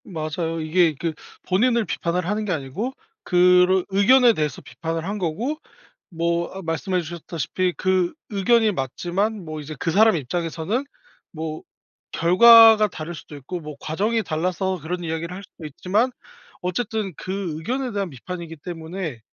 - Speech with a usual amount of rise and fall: Yes, average, 3.7 semitones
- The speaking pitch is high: No, medium, 180 Hz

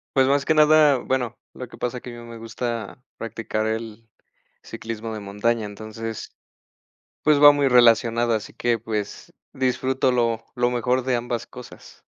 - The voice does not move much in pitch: Yes, narrow, 2.3 semitones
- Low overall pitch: Yes, low, 120 Hz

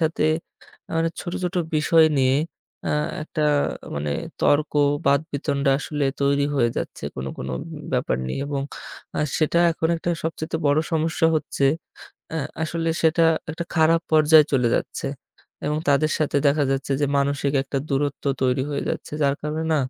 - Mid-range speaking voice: Yes, medium, 145 Hz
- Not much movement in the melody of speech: Yes, narrow, 2.3 semitones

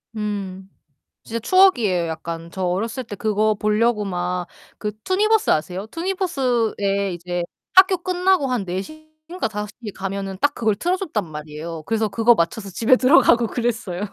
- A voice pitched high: Yes, high, 215 Hz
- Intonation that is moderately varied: No, wide, 6.0 semitones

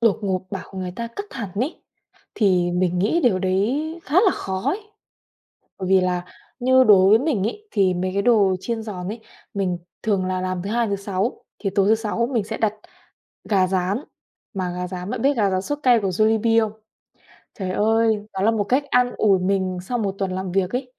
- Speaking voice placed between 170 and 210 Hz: Yes, high, 200 Hz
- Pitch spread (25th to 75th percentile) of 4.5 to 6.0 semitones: No, average, 3.8 semitones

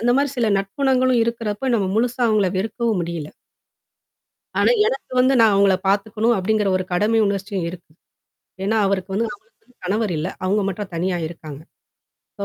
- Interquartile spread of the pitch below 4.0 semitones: Yes, average, 3.5 semitones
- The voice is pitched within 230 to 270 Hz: No, high, 210 Hz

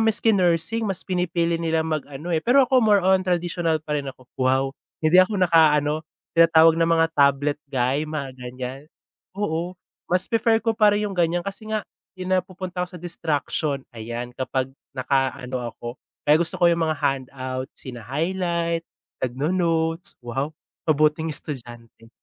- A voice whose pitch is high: No, medium, 160 Hz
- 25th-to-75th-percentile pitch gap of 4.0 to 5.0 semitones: Yes, average, 4.7 semitones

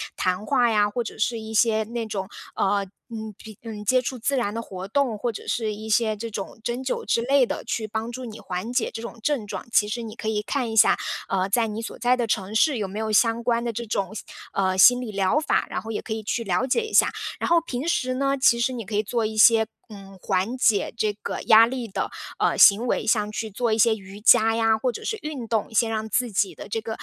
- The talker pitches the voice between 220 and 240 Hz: Yes, high, 225 Hz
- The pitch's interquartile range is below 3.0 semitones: Yes, narrow, 2.4 semitones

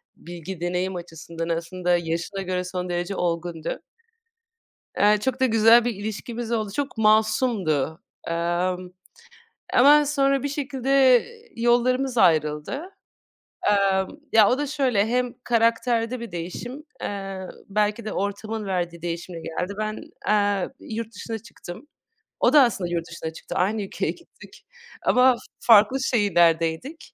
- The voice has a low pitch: No, high, 205 Hz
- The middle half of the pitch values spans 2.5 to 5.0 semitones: No, wide, 5.4 semitones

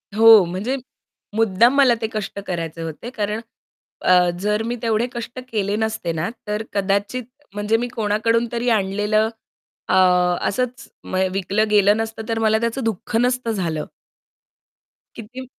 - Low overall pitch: No, high, 220 Hz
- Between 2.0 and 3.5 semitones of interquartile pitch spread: Yes, narrow, 2.6 semitones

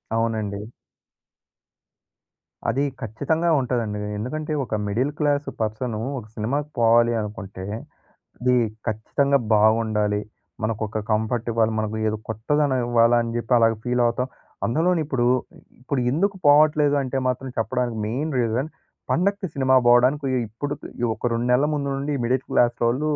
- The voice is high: No, low, 120 Hz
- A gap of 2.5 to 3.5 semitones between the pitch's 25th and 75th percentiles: No, average, 4.2 semitones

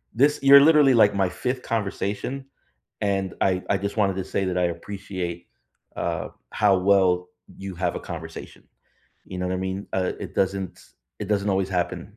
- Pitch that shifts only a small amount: Yes, narrow, 2.1 semitones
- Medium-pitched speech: No, very low, 95 Hz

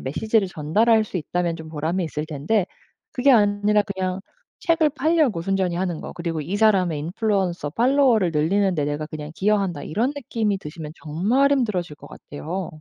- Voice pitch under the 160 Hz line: No, high, 190 Hz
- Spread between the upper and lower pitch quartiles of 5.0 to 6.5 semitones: Yes, wide, 5.4 semitones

